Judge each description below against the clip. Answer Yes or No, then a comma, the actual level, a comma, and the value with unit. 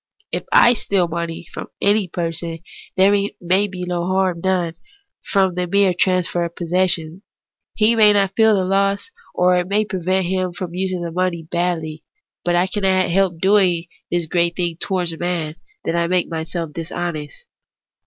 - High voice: No, medium, 180 Hz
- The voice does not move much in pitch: Yes, narrow, 2.0 semitones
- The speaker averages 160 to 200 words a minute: Yes, average, 165 wpm